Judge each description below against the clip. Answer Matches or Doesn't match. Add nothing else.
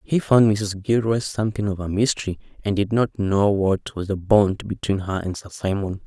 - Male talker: Matches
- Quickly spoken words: Matches